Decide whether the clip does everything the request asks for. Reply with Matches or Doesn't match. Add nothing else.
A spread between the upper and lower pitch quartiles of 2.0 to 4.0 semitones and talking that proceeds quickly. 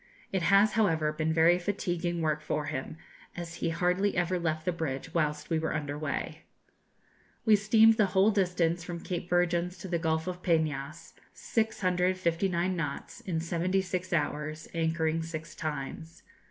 Doesn't match